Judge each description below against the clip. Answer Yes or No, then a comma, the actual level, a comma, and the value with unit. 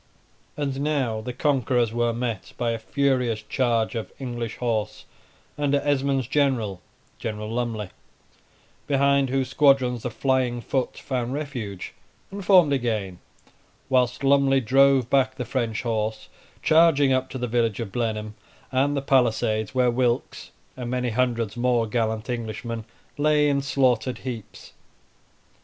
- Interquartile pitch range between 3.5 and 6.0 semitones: No, average, 3.1 semitones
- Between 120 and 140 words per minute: Yes, slow, 135 wpm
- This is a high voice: No, low, 125 Hz